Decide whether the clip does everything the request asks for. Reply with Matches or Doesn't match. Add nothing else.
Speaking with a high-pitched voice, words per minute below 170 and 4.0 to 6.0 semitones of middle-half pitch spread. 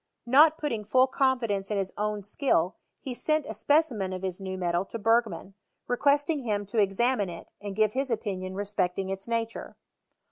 Doesn't match